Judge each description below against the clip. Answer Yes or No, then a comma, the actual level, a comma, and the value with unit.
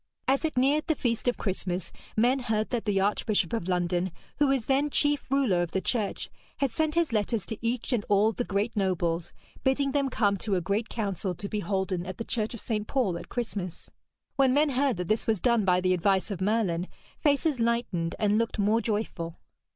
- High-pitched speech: Yes, high, 215 Hz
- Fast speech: Yes, fast, 210 wpm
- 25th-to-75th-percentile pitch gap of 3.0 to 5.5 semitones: Yes, average, 4.9 semitones